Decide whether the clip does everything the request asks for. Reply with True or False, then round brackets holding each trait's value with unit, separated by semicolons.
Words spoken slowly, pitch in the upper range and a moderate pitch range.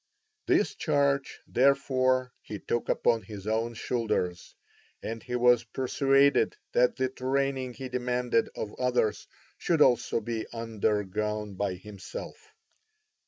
False (120 wpm; 125 Hz; 3.3 semitones)